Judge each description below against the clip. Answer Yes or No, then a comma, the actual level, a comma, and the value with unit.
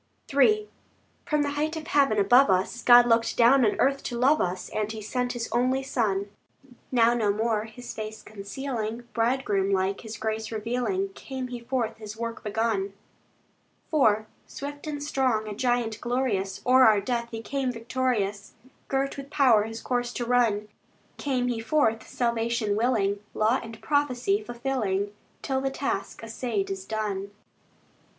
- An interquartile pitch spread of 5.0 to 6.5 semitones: No, average, 3.5 semitones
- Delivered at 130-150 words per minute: No, average, 160 wpm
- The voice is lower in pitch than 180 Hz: No, high, 235 Hz